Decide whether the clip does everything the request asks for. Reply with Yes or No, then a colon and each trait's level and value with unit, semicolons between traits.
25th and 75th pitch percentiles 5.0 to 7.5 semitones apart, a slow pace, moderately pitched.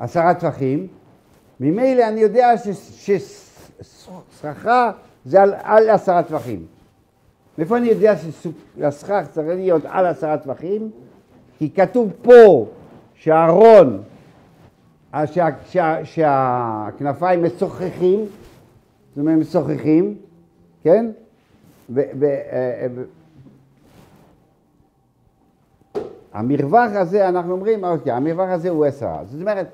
Yes: wide, 5.6 semitones; slow, 80 wpm; medium, 175 Hz